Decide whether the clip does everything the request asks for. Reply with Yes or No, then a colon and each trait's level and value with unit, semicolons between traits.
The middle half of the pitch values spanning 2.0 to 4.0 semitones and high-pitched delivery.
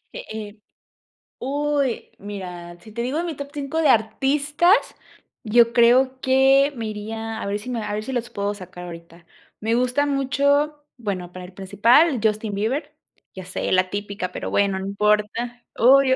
No: average, 5.1 semitones; high, 230 Hz